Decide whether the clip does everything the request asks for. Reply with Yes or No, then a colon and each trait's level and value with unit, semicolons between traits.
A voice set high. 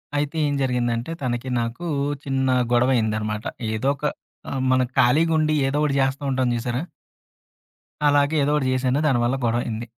No: low, 130 Hz